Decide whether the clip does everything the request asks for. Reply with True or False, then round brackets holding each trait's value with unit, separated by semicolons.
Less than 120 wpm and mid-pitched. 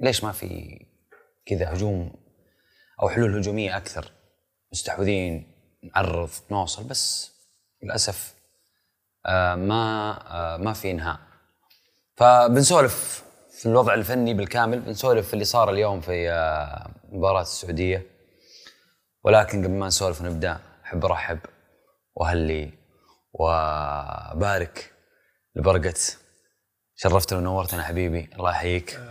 False (95 wpm; 95 Hz)